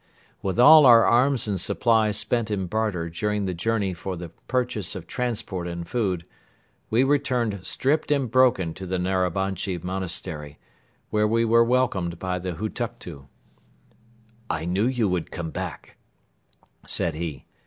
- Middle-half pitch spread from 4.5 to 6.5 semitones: Yes, average, 4.8 semitones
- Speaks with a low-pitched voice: Yes, low, 100 Hz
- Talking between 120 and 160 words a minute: Yes, average, 145 wpm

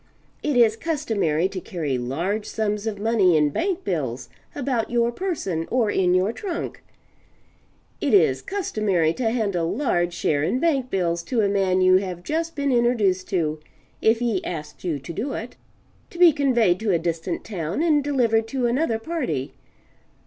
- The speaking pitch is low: No, high, 215 Hz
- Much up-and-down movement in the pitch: Yes, wide, 6.4 semitones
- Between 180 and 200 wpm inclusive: No, average, 170 wpm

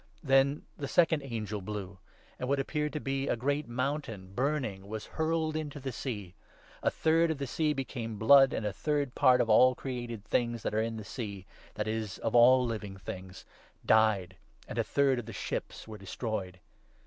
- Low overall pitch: Yes, low, 120 Hz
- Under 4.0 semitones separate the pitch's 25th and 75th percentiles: No, average, 4.7 semitones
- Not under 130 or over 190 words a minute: No, fast, 205 wpm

